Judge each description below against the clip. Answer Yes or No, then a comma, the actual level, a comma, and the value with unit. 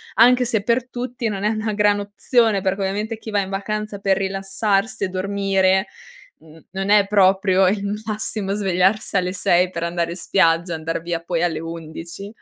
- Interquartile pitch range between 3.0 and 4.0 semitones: No, narrow, 2.5 semitones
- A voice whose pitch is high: Yes, high, 195 Hz